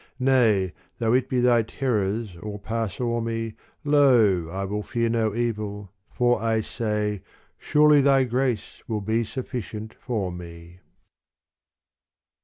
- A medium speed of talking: No, slow, 130 wpm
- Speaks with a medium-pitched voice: No, low, 115 Hz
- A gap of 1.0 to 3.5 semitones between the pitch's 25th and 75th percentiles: Yes, average, 3.0 semitones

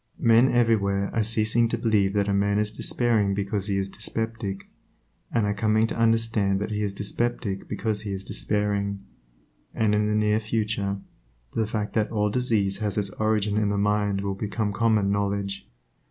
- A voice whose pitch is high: No, low, 105 Hz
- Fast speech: No, average, 180 wpm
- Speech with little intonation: Yes, narrow, 1.8 semitones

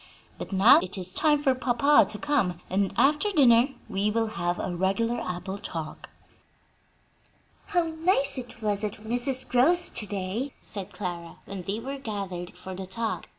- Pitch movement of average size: No, wide, 5.9 semitones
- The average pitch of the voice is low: No, high, 215 Hz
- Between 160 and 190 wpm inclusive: Yes, average, 165 wpm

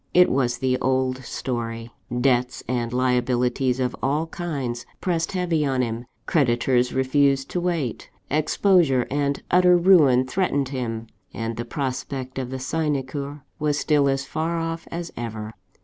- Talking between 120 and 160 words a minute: Yes, average, 145 wpm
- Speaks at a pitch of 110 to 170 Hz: Yes, low, 135 Hz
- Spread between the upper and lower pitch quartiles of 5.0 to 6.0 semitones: No, average, 3.7 semitones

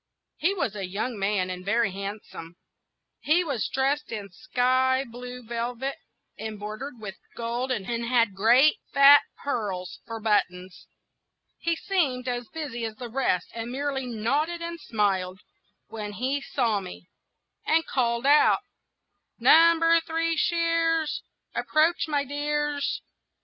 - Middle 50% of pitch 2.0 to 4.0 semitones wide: No, wide, 5.6 semitones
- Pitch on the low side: No, very high, 250 Hz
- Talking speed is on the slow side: Yes, slow, 130 wpm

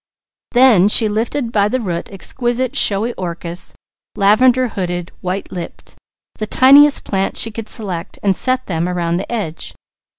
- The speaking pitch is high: Yes, high, 205 Hz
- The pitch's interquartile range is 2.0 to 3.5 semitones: No, average, 5.1 semitones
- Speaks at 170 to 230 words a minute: No, average, 145 wpm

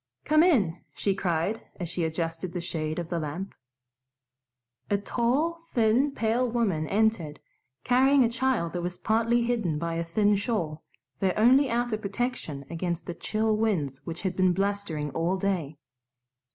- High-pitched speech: Yes, high, 195 Hz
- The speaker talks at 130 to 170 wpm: Yes, average, 155 wpm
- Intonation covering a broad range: Yes, wide, 5.7 semitones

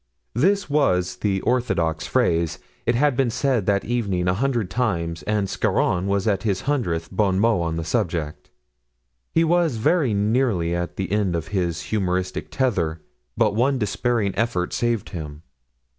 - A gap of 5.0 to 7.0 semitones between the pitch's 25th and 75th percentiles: Yes, wide, 5.5 semitones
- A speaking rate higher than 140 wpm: Yes, average, 155 wpm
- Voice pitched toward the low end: Yes, low, 100 Hz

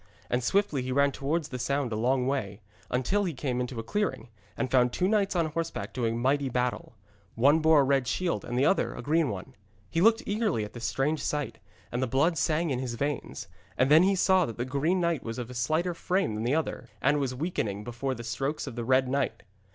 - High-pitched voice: No, low, 135 Hz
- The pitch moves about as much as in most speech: Yes, average, 4.7 semitones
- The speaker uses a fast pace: Yes, fast, 230 wpm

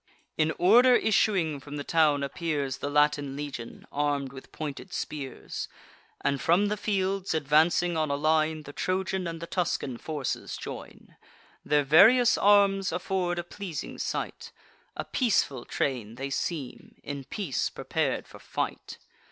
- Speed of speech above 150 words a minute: No, average, 145 wpm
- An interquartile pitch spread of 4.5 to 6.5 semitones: Yes, average, 4.8 semitones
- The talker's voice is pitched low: No, medium, 155 Hz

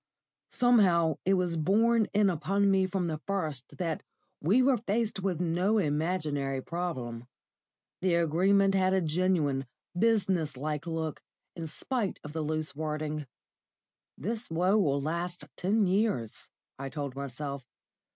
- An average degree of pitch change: Yes, average, 4.4 semitones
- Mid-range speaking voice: Yes, medium, 170 Hz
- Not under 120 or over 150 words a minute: Yes, slow, 135 wpm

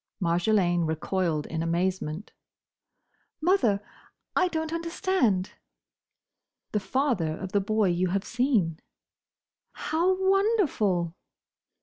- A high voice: Yes, high, 200 Hz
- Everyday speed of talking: No, slow, 85 wpm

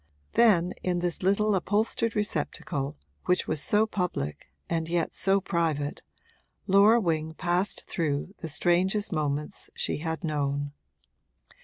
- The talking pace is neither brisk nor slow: No, slow, 125 wpm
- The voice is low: No, medium, 175 Hz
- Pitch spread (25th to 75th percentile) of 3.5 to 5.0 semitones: Yes, average, 4.2 semitones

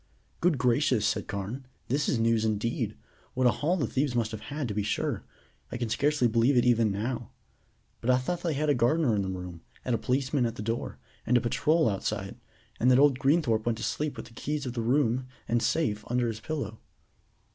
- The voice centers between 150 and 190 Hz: No, low, 120 Hz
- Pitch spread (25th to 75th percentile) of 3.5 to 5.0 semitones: Yes, average, 3.9 semitones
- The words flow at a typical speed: No, fast, 215 wpm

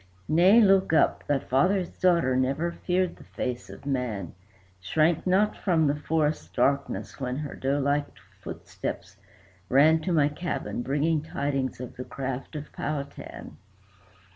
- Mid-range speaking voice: Yes, medium, 145 Hz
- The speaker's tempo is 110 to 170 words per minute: Yes, average, 140 wpm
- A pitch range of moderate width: Yes, average, 3.9 semitones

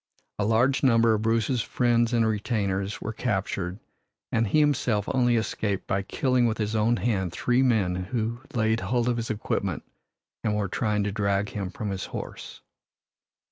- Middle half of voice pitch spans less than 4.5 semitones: Yes, average, 2.9 semitones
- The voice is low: Yes, low, 110 Hz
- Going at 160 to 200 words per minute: Yes, average, 170 wpm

